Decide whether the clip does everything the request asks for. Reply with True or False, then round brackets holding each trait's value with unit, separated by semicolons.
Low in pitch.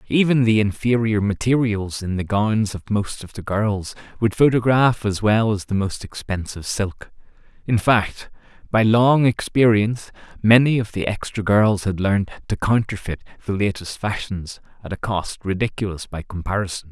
True (105 Hz)